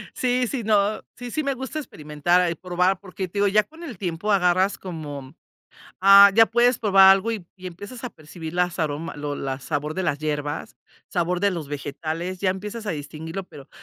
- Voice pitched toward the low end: No, medium, 180 Hz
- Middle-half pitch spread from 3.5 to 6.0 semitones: Yes, average, 4.7 semitones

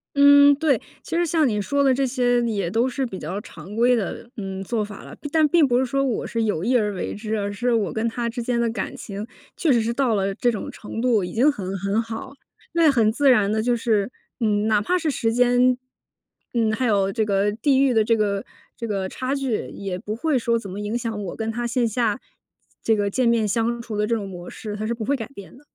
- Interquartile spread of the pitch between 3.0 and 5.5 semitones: Yes, average, 3.3 semitones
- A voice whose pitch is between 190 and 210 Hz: No, high, 230 Hz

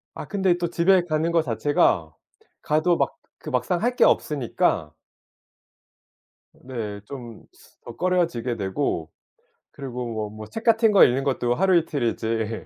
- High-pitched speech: No, low, 135 Hz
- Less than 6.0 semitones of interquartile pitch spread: No, wide, 7.4 semitones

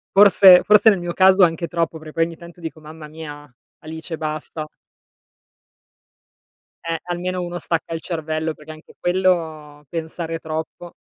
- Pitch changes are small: Yes, narrow, 2.0 semitones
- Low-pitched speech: No, medium, 165 Hz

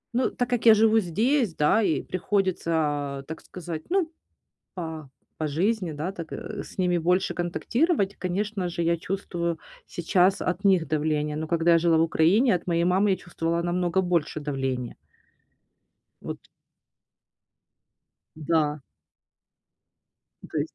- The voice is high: No, medium, 175 Hz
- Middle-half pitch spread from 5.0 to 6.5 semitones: No, average, 3.5 semitones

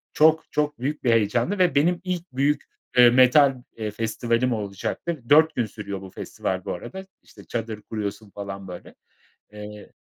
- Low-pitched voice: Yes, low, 120 Hz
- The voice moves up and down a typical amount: No, wide, 6.1 semitones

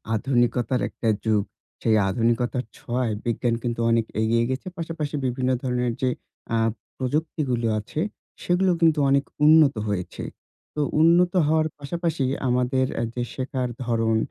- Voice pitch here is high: No, low, 125 Hz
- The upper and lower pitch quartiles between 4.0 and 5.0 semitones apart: Yes, average, 4.4 semitones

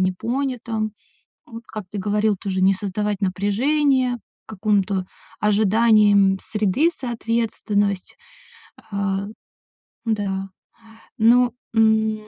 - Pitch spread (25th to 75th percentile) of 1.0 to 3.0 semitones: Yes, narrow, 2.4 semitones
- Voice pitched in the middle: No, high, 210 Hz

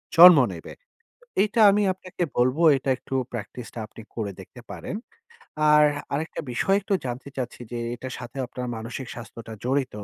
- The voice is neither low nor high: No, low, 125 Hz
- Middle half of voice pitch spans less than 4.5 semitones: No, average, 4.8 semitones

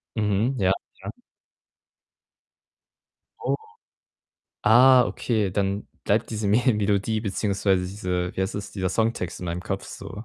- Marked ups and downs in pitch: No, average, 2.7 semitones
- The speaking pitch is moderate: No, low, 100 Hz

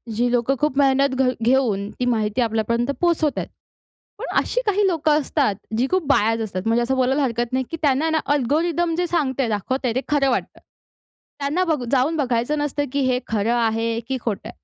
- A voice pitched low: No, very high, 265 Hz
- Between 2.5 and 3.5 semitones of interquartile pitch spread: No, average, 4.2 semitones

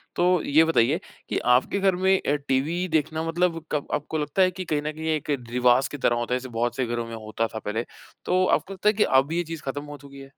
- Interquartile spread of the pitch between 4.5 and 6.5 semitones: Yes, average, 5.2 semitones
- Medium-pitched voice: Yes, medium, 150 Hz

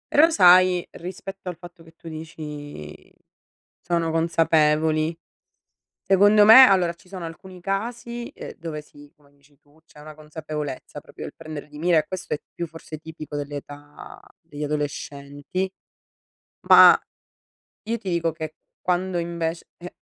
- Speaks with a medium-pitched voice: Yes, medium, 165 Hz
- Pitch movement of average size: Yes, average, 3.2 semitones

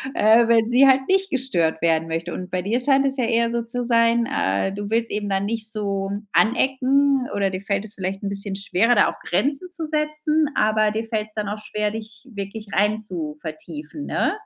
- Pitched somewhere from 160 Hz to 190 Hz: No, high, 220 Hz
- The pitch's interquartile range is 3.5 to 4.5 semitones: Yes, average, 4.0 semitones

